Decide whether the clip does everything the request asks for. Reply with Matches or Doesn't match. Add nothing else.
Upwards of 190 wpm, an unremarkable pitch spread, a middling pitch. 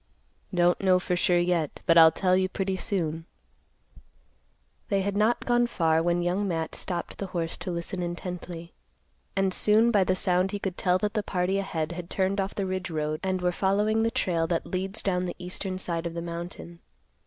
Doesn't match